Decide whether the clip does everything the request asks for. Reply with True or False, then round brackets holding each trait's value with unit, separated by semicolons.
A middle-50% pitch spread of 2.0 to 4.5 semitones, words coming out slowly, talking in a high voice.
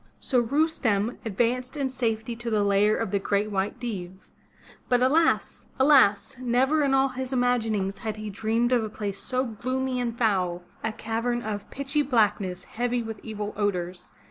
False (3.6 semitones; 170 wpm; 225 Hz)